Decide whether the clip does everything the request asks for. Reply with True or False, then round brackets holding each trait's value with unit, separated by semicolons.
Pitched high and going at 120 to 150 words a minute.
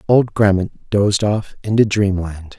False (100 Hz; 140 wpm)